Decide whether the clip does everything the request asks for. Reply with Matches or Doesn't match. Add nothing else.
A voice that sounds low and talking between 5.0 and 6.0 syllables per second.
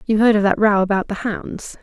Doesn't match